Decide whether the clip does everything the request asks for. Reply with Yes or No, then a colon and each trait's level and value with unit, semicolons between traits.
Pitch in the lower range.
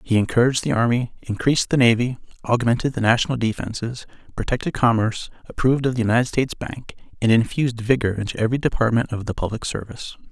Yes: low, 120 Hz